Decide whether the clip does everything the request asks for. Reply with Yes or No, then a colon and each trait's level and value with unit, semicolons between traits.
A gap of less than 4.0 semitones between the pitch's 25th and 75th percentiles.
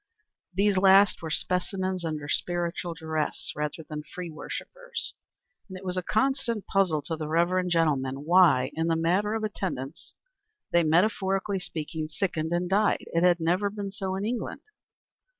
Yes: average, 3.4 semitones